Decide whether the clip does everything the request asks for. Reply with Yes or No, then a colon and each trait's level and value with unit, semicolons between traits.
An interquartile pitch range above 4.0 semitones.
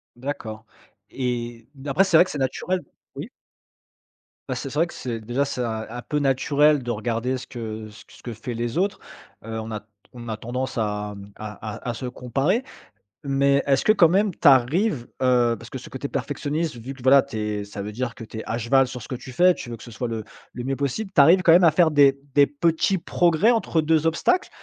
Yes: average, 4.4 semitones